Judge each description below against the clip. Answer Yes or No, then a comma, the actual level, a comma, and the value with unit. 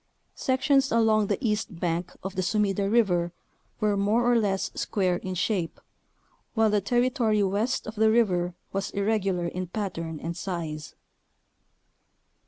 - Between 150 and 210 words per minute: No, average, 140 wpm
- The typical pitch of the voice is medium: No, high, 200 Hz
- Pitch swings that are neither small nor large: Yes, average, 3.6 semitones